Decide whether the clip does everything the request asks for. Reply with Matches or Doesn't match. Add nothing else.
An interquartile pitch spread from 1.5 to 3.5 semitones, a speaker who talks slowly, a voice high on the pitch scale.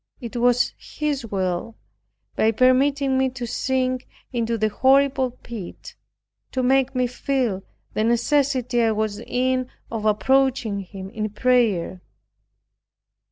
Matches